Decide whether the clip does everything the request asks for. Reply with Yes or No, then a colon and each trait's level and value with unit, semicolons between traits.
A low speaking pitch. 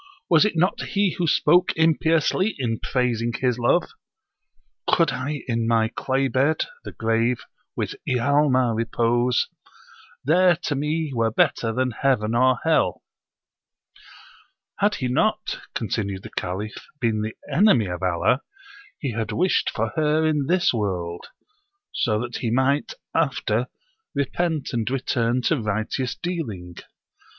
Yes: low, 125 Hz